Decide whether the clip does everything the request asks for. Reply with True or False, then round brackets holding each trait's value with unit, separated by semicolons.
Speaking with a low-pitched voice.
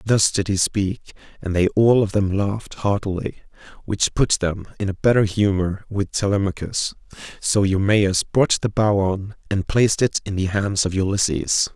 True (100 Hz)